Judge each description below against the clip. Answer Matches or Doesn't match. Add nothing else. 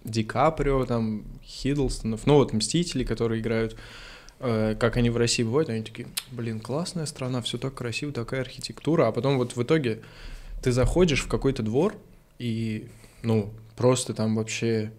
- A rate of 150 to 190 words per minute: Matches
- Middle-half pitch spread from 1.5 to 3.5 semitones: Matches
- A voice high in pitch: Doesn't match